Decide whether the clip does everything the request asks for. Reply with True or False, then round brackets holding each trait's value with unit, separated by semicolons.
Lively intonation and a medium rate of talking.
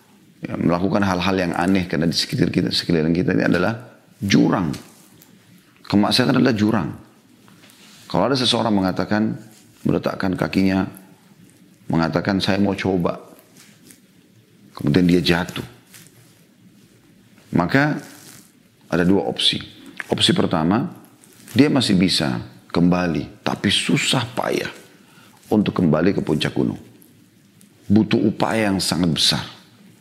False (3.2 semitones; 105 wpm)